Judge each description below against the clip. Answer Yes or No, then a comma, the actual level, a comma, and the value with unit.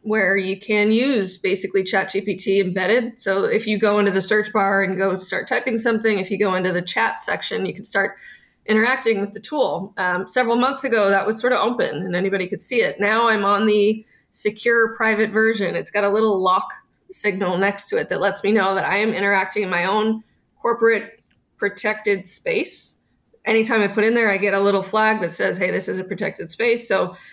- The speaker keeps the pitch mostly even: Yes, narrow, 2.3 semitones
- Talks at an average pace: No, fast, 215 wpm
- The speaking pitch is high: Yes, high, 205 Hz